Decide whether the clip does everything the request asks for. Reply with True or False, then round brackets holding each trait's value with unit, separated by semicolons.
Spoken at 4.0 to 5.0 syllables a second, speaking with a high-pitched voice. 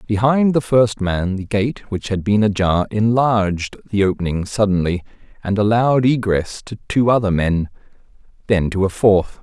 False (4.7 syllables/s; 105 Hz)